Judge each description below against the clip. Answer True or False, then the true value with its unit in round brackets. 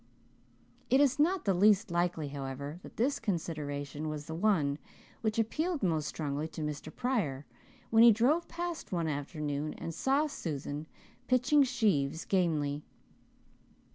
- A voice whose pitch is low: False (170 Hz)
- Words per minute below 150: True (140 wpm)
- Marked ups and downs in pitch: True (8.2 semitones)